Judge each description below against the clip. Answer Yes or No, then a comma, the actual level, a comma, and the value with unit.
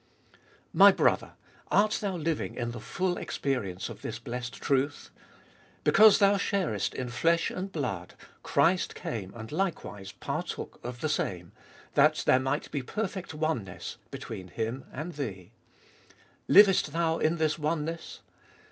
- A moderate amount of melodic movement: No, wide, 6.3 semitones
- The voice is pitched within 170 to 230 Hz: No, medium, 150 Hz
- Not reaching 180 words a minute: Yes, average, 140 wpm